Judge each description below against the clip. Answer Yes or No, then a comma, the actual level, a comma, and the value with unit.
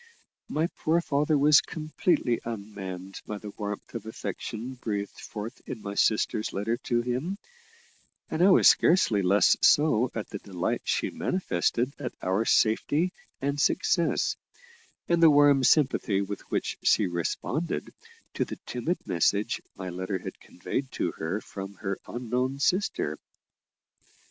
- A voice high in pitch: No, low, 115 Hz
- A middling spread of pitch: No, wide, 6.4 semitones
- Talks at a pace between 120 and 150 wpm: Yes, average, 140 wpm